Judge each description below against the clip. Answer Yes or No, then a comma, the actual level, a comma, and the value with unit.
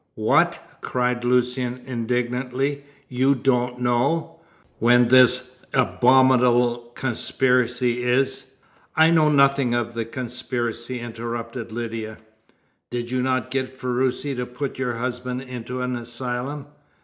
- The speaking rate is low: Yes, slow, 115 wpm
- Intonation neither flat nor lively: No, narrow, 1.4 semitones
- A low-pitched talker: Yes, low, 125 Hz